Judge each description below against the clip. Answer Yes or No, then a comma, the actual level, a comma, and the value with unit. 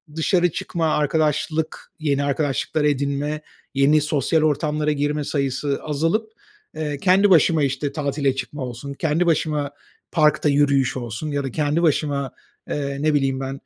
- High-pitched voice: No, medium, 145 Hz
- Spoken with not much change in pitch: Yes, narrow, 1.9 semitones